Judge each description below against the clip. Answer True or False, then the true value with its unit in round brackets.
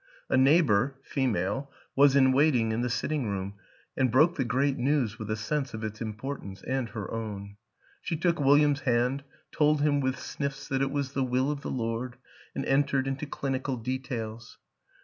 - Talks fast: False (185 wpm)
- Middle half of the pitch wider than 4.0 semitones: False (3.7 semitones)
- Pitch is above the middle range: False (130 Hz)